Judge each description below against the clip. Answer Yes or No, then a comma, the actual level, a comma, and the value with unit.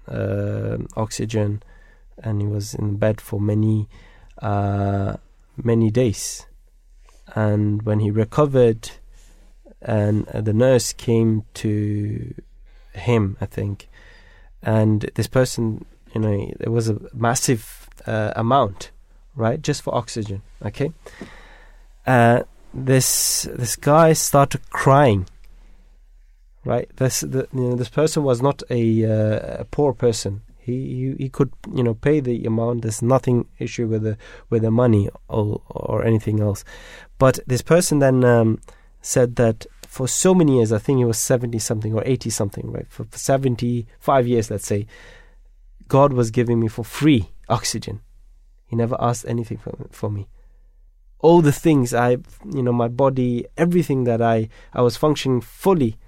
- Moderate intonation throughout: Yes, average, 3.4 semitones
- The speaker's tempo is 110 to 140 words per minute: No, average, 150 wpm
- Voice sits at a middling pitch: No, low, 115 Hz